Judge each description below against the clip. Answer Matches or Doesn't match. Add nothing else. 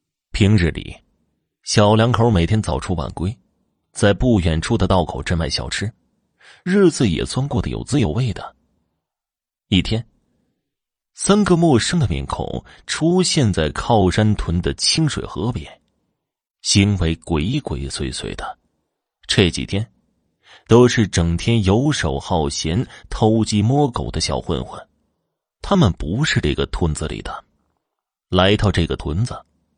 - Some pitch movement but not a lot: Doesn't match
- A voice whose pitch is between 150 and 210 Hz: Doesn't match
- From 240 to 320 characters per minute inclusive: Doesn't match